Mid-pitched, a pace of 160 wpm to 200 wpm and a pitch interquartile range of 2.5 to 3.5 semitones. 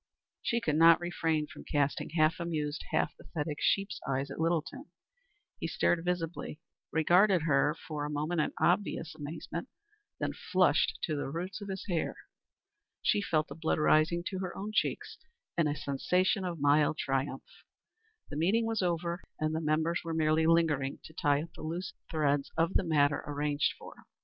Yes: medium, 160 Hz; average, 170 wpm; average, 2.8 semitones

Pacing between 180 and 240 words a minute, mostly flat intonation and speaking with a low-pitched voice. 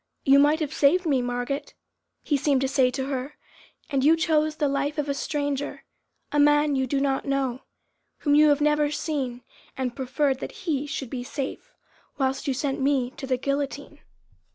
No: average, 185 wpm; narrow, 1.9 semitones; very high, 280 Hz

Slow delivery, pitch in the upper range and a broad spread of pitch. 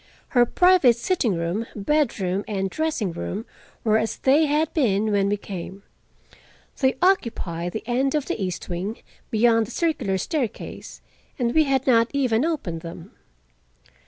No: average, 150 wpm; high, 230 Hz; wide, 6.0 semitones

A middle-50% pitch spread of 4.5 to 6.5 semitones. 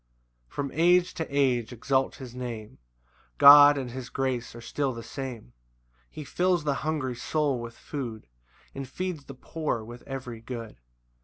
No: average, 3.4 semitones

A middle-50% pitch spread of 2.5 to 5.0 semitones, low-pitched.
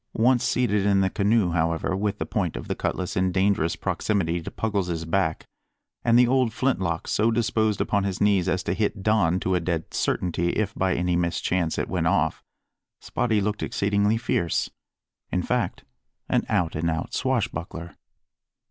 Yes: average, 3.8 semitones; very low, 95 Hz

